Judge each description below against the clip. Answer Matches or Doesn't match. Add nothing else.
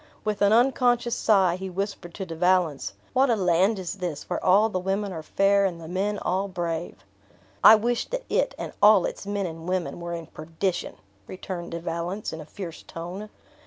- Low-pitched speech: Doesn't match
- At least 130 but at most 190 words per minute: Doesn't match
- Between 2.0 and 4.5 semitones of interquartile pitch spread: Matches